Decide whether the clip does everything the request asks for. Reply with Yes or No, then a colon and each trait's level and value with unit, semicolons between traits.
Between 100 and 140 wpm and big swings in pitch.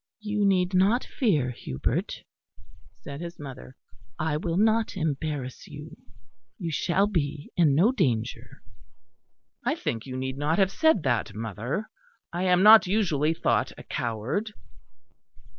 Yes: slow, 135 wpm; wide, 6.8 semitones